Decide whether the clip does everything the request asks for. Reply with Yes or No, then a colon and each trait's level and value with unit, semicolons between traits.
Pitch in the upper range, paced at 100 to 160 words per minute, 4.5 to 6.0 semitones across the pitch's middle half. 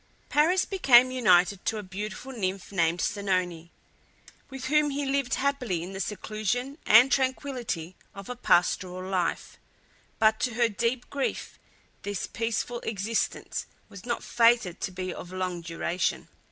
Yes: high, 215 Hz; average, 140 wpm; wide, 5.4 semitones